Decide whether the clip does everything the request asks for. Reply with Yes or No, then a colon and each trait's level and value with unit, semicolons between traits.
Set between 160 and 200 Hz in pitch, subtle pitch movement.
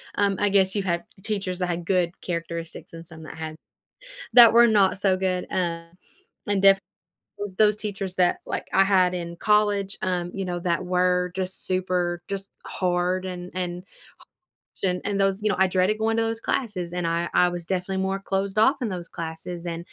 Yes: medium, 185 Hz; narrow, 2.0 semitones